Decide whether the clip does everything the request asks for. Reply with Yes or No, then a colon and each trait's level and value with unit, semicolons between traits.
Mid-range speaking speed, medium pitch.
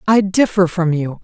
Yes: average, 195 wpm; medium, 180 Hz